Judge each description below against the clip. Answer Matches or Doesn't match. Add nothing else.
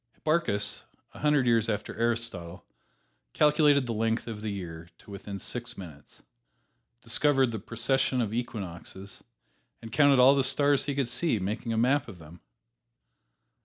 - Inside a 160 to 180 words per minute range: Doesn't match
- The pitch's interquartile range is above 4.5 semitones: Matches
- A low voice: Matches